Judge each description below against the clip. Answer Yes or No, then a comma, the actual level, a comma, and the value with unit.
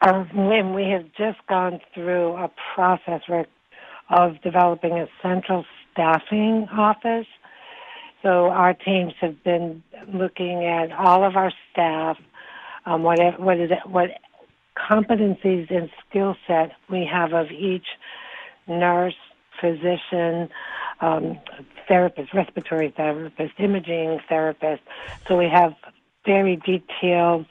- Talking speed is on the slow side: Yes, slow, 120 wpm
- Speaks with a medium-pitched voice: Yes, medium, 180 Hz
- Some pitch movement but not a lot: No, narrow, 2.1 semitones